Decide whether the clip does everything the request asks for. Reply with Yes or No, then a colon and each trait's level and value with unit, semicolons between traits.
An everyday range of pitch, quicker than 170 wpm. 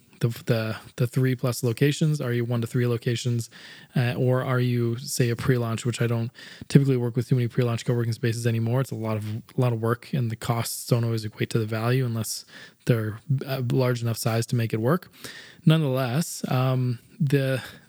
No: narrow, 2.1 semitones; average, 200 wpm